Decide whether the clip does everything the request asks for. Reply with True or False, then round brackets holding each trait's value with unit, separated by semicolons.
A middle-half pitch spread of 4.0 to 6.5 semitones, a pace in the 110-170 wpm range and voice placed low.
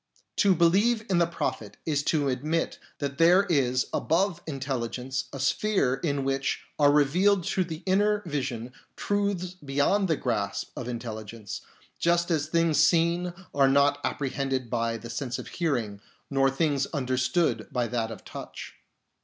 False (5.1 semitones; 155 wpm; 145 Hz)